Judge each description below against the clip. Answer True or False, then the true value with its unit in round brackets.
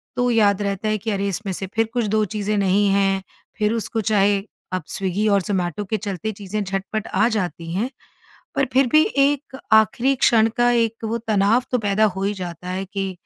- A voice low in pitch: False (205 Hz)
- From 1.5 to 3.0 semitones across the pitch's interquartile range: True (2.4 semitones)